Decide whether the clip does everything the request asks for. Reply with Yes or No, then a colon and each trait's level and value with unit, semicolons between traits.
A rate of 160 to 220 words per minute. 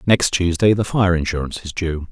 Yes: average, 200 wpm